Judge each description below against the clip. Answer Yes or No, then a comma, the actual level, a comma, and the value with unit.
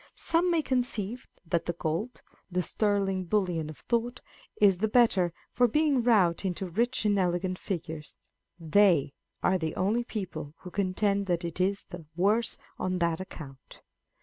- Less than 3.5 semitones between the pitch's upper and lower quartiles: No, average, 4.2 semitones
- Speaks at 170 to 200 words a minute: No, average, 155 wpm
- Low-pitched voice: No, high, 190 Hz